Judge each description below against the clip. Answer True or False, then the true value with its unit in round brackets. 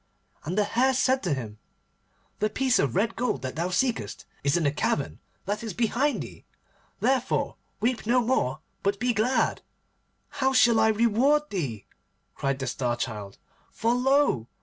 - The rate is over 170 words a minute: False (165 wpm)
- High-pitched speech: True (215 Hz)